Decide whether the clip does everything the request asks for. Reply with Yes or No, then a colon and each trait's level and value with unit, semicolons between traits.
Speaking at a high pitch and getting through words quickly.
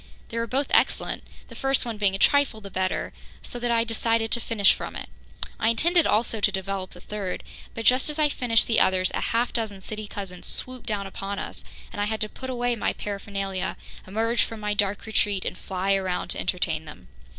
Yes: high, 215 Hz; fast, 215 wpm